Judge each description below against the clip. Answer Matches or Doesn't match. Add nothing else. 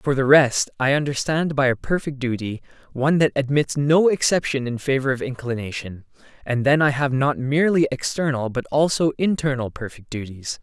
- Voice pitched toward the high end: Doesn't match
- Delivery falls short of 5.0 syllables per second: Doesn't match